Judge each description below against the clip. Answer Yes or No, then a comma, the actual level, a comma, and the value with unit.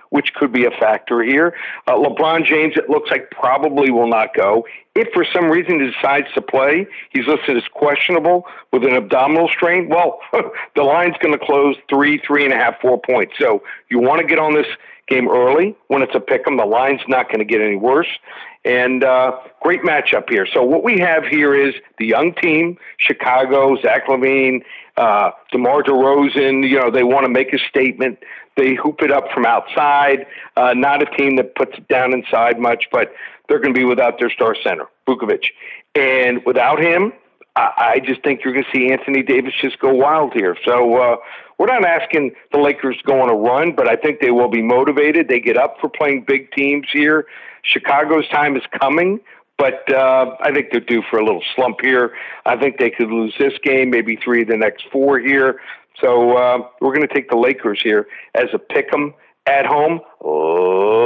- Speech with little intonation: No, average, 3.4 semitones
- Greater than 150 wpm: Yes, fast, 205 wpm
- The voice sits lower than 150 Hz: Yes, medium, 140 Hz